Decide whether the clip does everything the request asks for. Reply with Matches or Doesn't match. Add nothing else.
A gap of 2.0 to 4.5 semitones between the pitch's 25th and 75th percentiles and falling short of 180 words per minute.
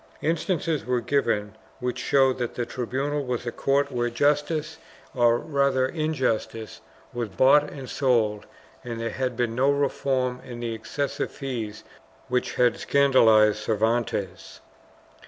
Matches